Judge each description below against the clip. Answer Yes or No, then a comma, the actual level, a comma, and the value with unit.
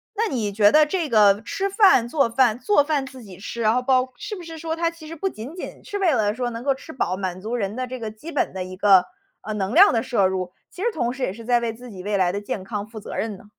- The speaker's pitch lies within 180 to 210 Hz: No, high, 240 Hz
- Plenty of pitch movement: Yes, wide, 6.7 semitones